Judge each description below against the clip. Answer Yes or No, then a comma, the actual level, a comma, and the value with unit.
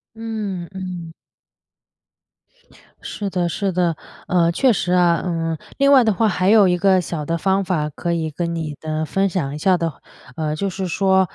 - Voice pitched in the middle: Yes, medium, 180 Hz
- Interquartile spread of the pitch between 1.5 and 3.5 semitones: Yes, average, 2.7 semitones